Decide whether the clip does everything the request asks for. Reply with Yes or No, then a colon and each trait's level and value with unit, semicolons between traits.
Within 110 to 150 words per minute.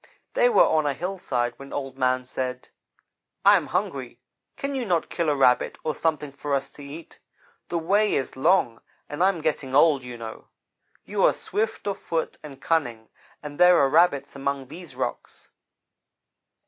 No: average, 175 wpm